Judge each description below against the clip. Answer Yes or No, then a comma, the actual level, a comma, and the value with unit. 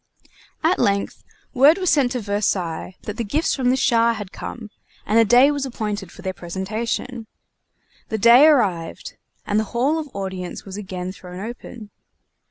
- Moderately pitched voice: No, high, 220 Hz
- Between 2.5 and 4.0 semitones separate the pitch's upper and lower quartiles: No, average, 4.6 semitones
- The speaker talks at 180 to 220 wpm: No, average, 170 wpm